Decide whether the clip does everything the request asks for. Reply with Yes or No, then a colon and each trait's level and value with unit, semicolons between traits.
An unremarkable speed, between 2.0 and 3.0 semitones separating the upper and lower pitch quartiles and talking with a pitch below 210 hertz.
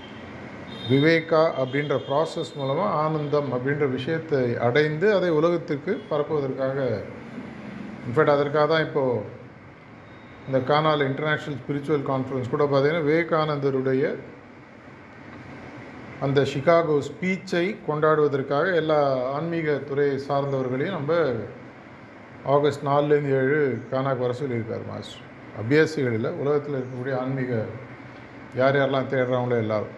Yes: average, 95 wpm; average, 2.7 semitones; medium, 140 Hz